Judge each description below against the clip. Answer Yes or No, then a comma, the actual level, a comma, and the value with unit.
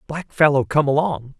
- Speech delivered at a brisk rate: No, average, 175 wpm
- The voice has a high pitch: No, medium, 145 Hz